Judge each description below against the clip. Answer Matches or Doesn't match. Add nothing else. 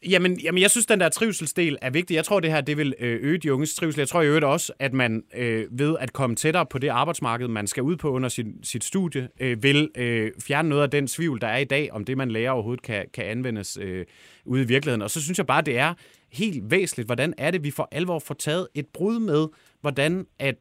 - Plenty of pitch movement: Doesn't match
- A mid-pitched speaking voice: Matches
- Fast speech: Matches